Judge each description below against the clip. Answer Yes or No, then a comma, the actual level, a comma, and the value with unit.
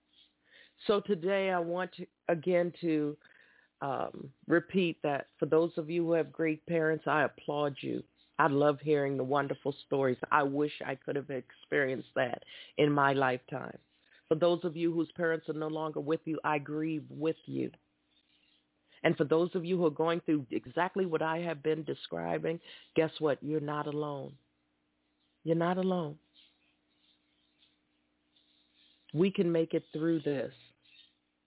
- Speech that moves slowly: No, average, 155 wpm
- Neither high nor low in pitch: Yes, medium, 150 Hz